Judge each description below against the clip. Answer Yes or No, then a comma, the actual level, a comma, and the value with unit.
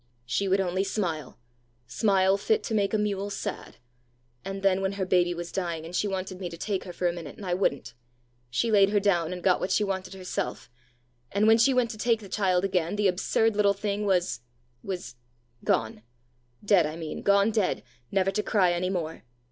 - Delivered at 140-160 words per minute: No, fast, 205 wpm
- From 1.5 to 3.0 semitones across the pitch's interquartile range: Yes, narrow, 2.4 semitones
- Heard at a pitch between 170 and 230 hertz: Yes, high, 190 Hz